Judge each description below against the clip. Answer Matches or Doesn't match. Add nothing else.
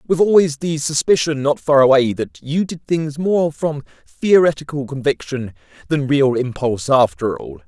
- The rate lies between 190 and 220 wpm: Doesn't match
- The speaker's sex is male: Matches